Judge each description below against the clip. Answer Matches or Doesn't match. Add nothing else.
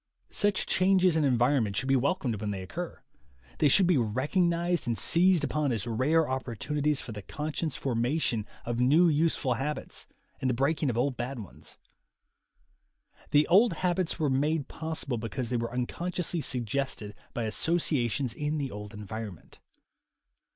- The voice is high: Doesn't match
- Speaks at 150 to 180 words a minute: Matches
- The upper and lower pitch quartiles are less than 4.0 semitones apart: Doesn't match